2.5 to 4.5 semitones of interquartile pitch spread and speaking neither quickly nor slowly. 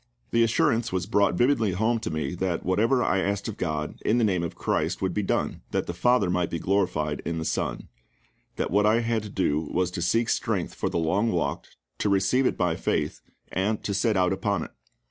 No: average, 4.1 semitones; fast, 220 wpm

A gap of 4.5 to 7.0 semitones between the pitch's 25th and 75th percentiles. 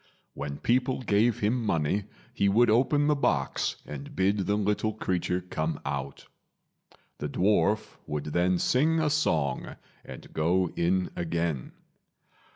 Yes: wide, 5.6 semitones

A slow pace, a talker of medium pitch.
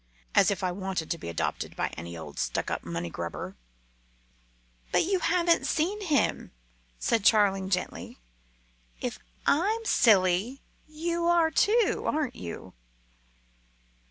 No: slow, 130 wpm; high, 220 Hz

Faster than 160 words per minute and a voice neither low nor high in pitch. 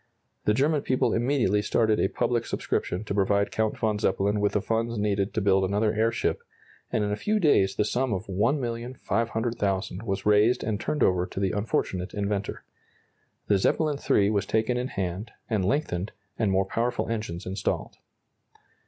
No: average, 170 wpm; low, 105 Hz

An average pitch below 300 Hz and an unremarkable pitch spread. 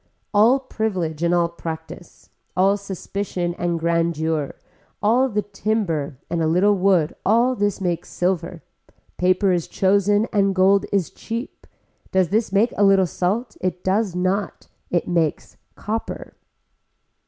Yes: high, 190 Hz; average, 3.2 semitones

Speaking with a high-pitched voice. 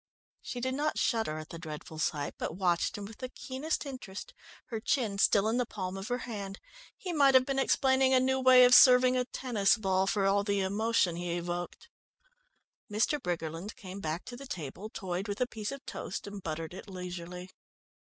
Yes: high, 205 Hz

